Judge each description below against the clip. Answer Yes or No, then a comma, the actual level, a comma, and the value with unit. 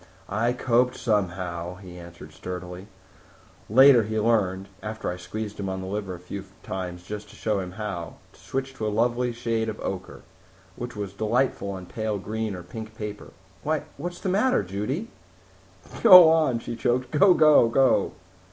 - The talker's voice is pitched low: Yes, low, 105 Hz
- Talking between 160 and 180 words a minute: Yes, average, 170 wpm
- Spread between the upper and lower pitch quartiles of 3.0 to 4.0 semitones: No, average, 4.4 semitones